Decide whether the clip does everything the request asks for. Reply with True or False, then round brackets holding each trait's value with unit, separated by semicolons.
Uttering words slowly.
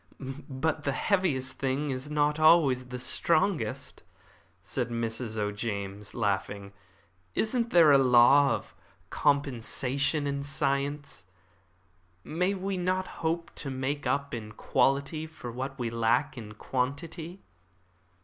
True (120 wpm)